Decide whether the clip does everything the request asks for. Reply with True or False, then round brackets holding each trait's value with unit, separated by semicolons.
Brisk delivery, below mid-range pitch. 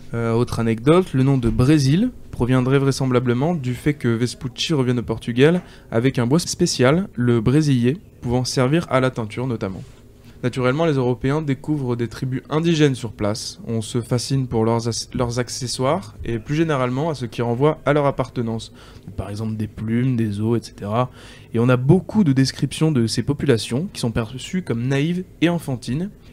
False (175 wpm; 125 Hz)